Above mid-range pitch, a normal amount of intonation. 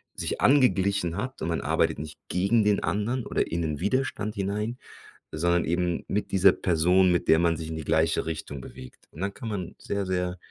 No: very low, 90 Hz; average, 3.9 semitones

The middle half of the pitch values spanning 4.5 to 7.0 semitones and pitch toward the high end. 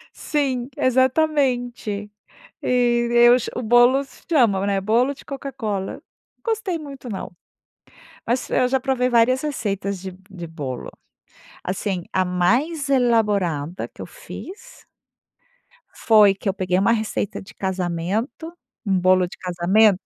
Yes: wide, 5.5 semitones; high, 230 Hz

